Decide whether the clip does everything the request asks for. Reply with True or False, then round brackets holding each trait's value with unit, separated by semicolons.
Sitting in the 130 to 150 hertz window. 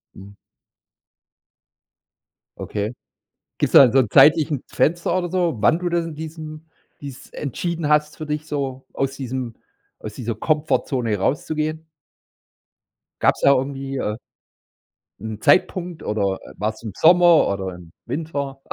True (140 Hz)